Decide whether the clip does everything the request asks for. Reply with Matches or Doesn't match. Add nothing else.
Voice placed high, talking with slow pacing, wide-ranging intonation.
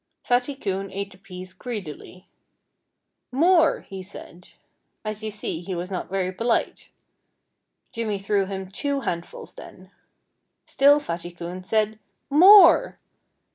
Doesn't match